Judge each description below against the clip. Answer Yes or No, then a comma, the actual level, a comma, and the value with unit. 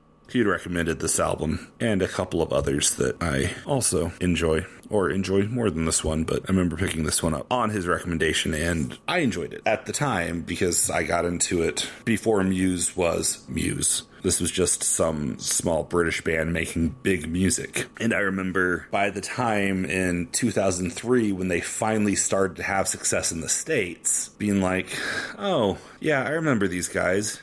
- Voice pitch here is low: Yes, very low, 90 Hz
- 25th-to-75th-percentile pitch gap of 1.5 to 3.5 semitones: Yes, narrow, 2.5 semitones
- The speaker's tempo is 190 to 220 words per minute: No, average, 175 wpm